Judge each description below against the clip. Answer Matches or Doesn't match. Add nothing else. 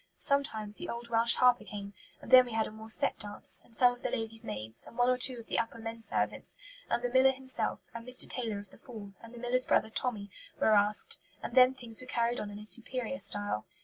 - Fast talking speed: Matches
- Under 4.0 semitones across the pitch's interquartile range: Matches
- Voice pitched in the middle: Doesn't match